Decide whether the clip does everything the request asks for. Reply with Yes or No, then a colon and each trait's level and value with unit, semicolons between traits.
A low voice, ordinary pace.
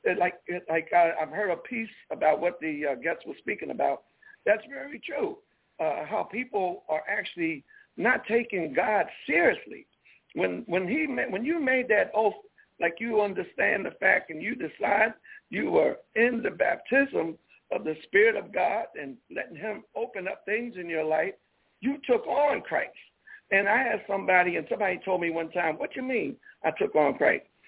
No: high, 210 Hz; average, 180 wpm